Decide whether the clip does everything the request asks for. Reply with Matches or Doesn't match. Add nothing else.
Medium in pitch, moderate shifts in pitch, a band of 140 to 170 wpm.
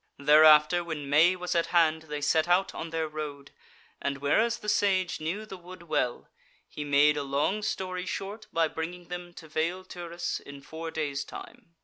Doesn't match